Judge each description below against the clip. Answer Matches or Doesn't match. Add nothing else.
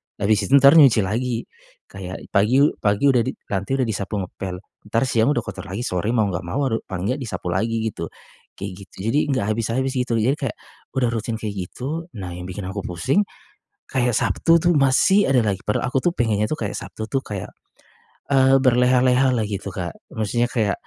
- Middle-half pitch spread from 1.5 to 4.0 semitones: Doesn't match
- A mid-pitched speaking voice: Doesn't match